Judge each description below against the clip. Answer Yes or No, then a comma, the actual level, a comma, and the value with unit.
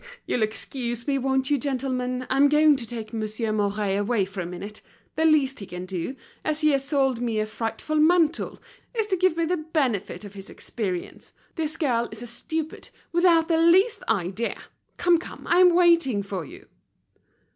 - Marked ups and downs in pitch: Yes, wide, 6.6 semitones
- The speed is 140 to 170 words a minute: No, average, 180 wpm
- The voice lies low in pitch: No, very high, 260 Hz